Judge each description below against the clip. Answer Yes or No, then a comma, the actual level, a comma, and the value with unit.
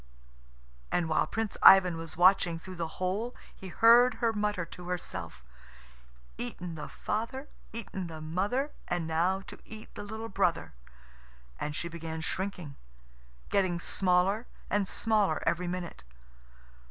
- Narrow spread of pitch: No, average, 3.8 semitones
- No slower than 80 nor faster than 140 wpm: Yes, slow, 135 wpm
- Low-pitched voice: No, medium, 185 Hz